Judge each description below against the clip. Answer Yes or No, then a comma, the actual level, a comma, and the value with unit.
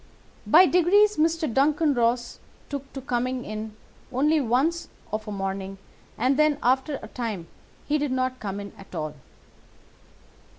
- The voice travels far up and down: Yes, wide, 5.7 semitones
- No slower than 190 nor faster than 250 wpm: No, average, 145 wpm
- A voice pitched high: Yes, very high, 255 Hz